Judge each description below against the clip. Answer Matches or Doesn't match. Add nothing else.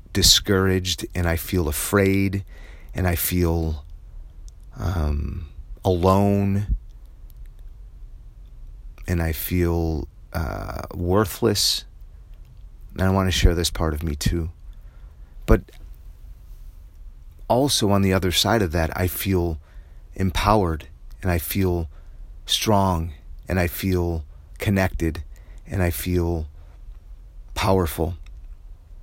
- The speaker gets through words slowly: Matches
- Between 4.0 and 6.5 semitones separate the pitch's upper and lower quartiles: Doesn't match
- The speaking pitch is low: Matches